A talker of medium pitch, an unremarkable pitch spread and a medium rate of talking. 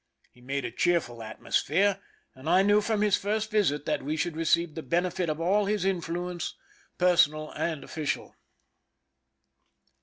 Yes: medium, 170 Hz; average, 4.0 semitones; average, 150 wpm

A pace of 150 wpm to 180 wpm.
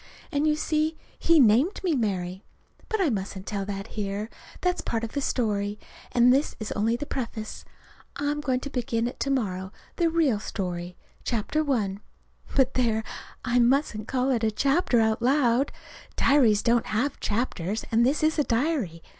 Yes: average, 170 wpm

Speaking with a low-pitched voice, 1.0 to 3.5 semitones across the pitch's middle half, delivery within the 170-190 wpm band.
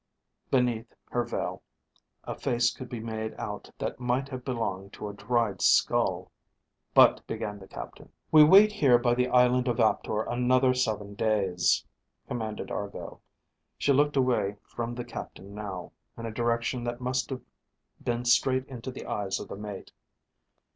No: low, 120 Hz; average, 3.0 semitones; average, 160 wpm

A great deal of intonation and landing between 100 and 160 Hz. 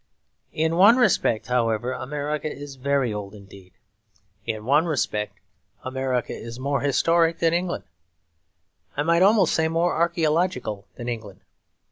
Yes: wide, 6.1 semitones; medium, 140 Hz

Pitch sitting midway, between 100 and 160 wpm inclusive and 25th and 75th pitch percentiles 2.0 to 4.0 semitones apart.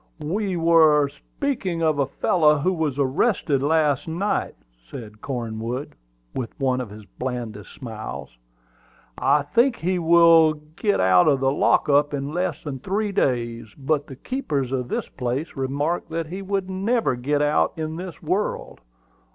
No: medium, 150 Hz; average, 155 wpm; average, 4.7 semitones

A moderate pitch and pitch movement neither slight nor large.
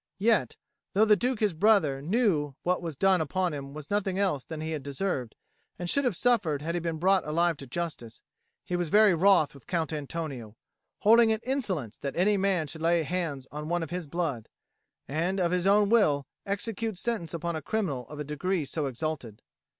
Yes: medium, 170 Hz; average, 4.8 semitones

